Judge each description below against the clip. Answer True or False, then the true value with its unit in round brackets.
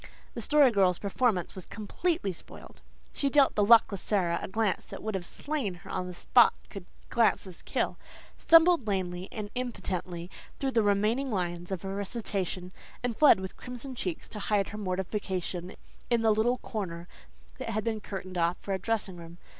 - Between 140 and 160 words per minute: False (180 wpm)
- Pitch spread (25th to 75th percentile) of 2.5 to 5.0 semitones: True (4.1 semitones)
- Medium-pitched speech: False (200 Hz)